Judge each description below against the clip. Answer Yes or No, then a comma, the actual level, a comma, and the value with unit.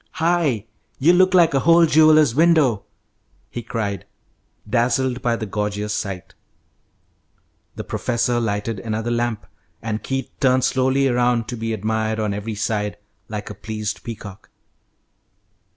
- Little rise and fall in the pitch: No, average, 3.9 semitones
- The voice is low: Yes, low, 115 Hz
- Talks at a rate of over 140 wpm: No, slow, 135 wpm